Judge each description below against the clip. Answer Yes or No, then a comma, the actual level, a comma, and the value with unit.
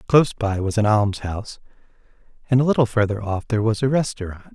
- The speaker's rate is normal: Yes, average, 185 wpm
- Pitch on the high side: No, low, 110 Hz